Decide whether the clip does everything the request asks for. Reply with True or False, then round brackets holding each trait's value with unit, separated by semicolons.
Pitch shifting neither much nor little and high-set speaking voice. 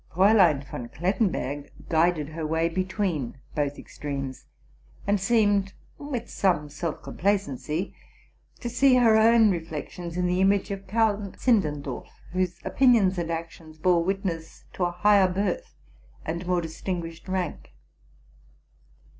False (3.8 semitones; 180 Hz)